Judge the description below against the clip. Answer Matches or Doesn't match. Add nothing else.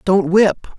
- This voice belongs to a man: Matches